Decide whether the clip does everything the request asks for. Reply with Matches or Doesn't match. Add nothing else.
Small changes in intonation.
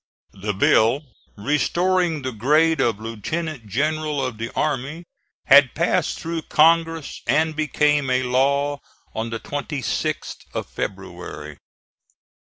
Doesn't match